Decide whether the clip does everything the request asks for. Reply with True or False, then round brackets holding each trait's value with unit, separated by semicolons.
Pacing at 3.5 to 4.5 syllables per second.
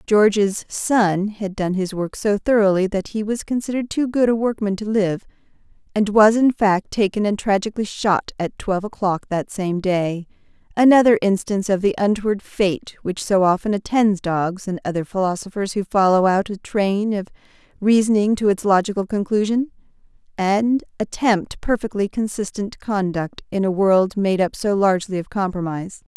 False (5.0 syllables/s)